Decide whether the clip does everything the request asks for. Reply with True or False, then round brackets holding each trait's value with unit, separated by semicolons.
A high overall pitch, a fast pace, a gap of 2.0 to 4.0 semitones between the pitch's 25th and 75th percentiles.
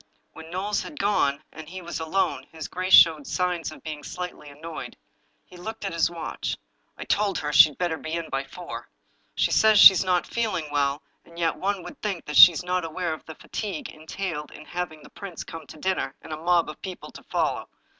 False (170 Hz; 220 wpm; 3.0 semitones)